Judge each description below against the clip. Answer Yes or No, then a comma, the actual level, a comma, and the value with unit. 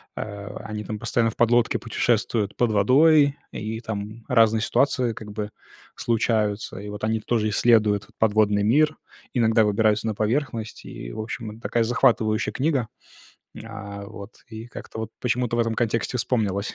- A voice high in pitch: No, low, 110 Hz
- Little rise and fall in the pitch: Yes, narrow, 2.0 semitones